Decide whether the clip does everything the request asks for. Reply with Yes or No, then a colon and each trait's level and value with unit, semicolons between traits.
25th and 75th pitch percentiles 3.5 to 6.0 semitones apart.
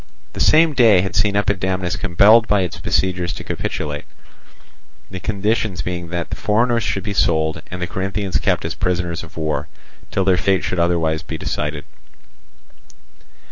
No: average, 3.0 semitones